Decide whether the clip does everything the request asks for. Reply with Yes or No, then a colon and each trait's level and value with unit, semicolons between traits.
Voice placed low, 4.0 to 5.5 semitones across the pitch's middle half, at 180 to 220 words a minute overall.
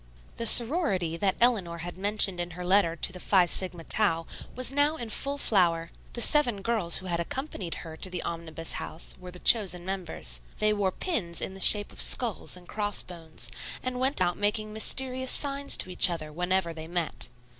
No: medium, 185 Hz; average, 4.9 semitones; average, 195 wpm